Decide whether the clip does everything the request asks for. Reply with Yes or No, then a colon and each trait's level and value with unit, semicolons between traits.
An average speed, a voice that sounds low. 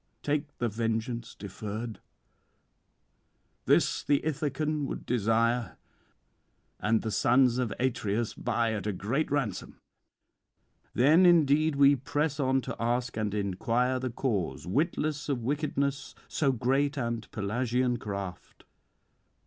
No: slow, 115 wpm; low, 125 Hz